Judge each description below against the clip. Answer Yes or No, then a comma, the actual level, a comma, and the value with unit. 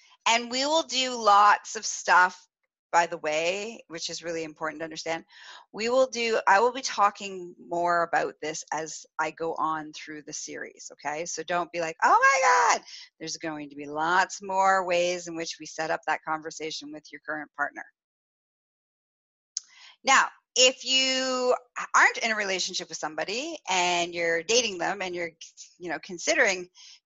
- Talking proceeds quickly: No, average, 170 wpm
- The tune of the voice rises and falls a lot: Yes, wide, 6.3 semitones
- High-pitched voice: No, medium, 175 Hz